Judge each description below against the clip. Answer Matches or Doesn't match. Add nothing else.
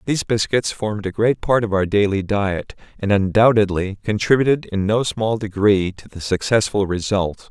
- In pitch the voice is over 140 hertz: Doesn't match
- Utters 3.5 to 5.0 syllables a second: Matches